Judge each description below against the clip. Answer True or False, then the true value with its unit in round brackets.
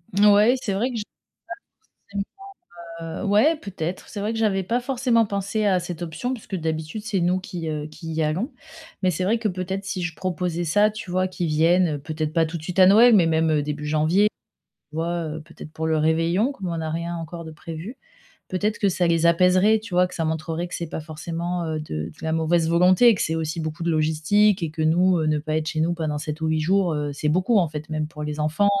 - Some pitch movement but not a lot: True (3.6 semitones)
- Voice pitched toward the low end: False (170 Hz)